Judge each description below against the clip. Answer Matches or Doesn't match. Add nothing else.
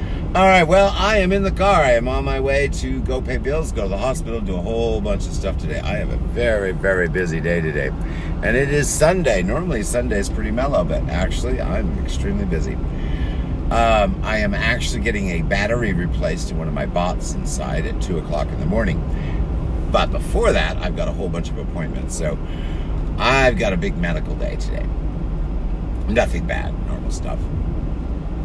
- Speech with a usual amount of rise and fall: Doesn't match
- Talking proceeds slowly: Doesn't match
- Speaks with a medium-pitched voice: Doesn't match